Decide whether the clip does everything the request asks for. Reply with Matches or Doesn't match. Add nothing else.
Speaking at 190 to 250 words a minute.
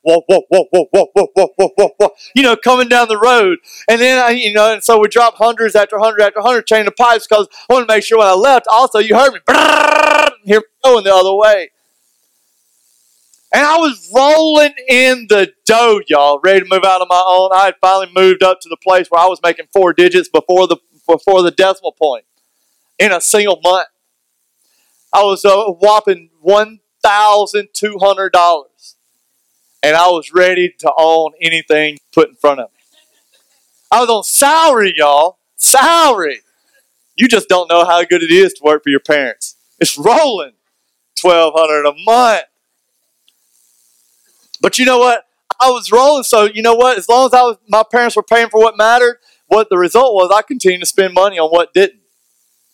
Doesn't match